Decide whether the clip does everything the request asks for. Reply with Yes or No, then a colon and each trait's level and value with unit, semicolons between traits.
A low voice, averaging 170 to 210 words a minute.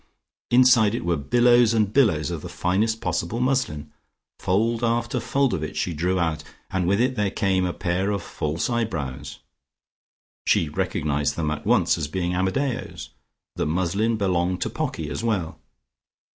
No: very low, 95 Hz; average, 160 wpm